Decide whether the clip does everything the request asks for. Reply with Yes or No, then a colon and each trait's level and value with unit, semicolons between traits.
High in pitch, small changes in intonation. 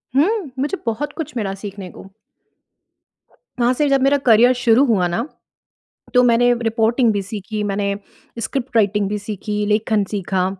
No: high, 225 Hz; average, 3.6 semitones